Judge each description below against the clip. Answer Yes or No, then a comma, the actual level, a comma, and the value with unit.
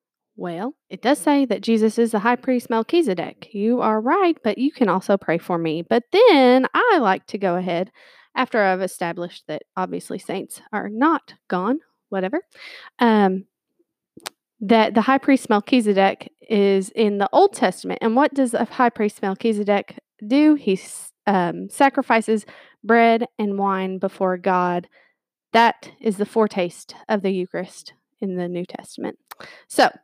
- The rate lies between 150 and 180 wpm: Yes, average, 155 wpm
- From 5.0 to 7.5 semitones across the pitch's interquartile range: Yes, wide, 5.4 semitones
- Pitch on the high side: Yes, high, 220 Hz